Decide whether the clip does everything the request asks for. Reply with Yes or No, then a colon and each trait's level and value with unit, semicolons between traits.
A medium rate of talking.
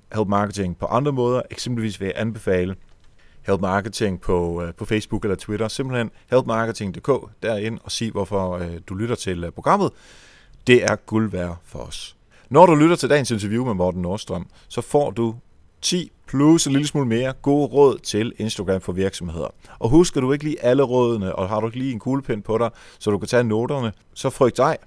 Yes: average, 195 wpm